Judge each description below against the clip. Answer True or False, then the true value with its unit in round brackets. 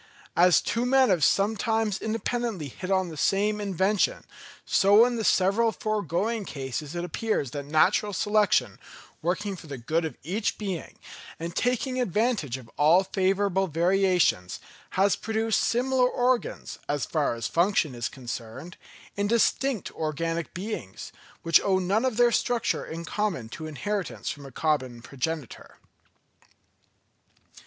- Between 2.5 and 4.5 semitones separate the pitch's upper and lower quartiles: False (5.6 semitones)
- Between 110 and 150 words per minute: True (140 wpm)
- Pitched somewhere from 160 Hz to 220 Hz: True (190 Hz)